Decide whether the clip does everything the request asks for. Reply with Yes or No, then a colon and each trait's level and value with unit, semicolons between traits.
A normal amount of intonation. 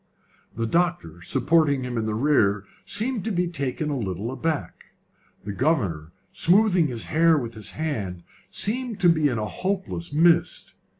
No: wide, 7.7 semitones